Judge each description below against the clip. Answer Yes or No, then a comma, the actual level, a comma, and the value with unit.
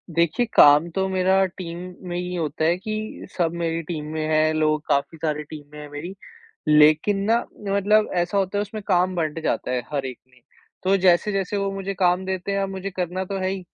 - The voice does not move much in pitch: No, average, 3.8 semitones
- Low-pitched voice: No, medium, 180 Hz